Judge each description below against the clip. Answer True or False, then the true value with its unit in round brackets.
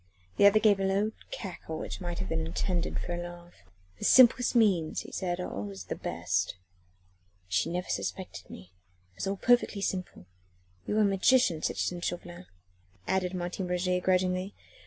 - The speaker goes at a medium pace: True (170 wpm)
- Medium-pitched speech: True (180 Hz)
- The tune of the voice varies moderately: False (2.2 semitones)